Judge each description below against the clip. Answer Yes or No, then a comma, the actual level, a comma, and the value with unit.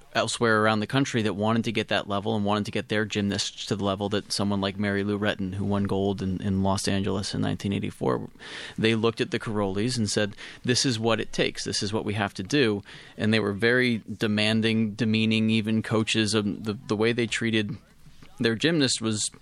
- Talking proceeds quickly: Yes, fast, 215 wpm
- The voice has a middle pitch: No, low, 110 Hz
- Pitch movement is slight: Yes, narrow, 2.1 semitones